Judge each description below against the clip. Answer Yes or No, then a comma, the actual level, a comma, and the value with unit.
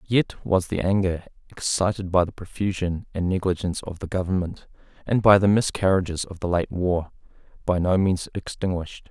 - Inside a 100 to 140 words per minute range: No, average, 165 wpm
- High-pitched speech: No, very low, 95 Hz